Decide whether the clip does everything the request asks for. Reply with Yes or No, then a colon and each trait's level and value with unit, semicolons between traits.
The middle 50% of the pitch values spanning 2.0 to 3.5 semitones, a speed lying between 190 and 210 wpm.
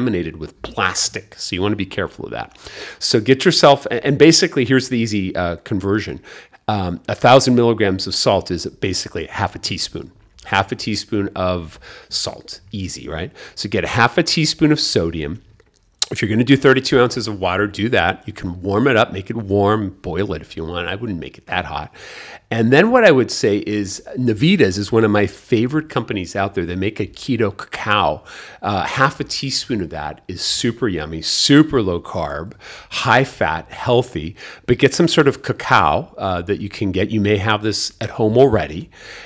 No: average, 4.6 semitones; average, 195 wpm